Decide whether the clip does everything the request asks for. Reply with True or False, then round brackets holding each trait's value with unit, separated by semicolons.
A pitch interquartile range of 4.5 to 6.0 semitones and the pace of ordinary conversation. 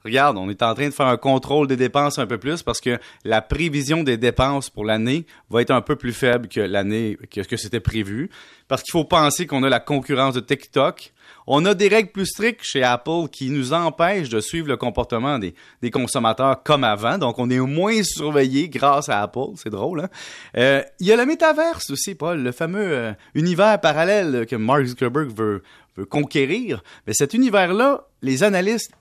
True (5.3 semitones; 205 wpm)